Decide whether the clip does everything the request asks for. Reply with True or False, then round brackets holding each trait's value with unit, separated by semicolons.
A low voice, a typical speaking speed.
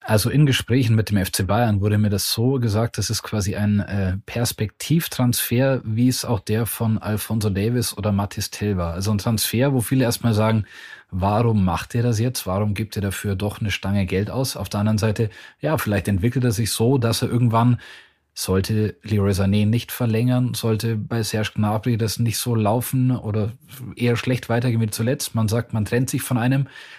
False (110 Hz; 195 wpm)